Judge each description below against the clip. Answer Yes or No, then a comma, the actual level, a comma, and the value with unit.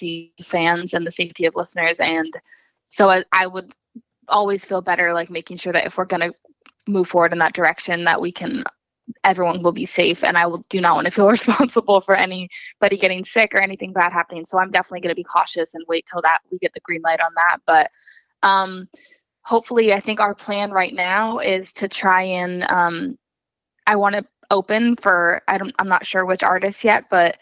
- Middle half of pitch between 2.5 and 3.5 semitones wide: Yes, average, 2.8 semitones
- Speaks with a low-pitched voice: No, medium, 185 Hz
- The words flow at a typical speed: No, fast, 210 wpm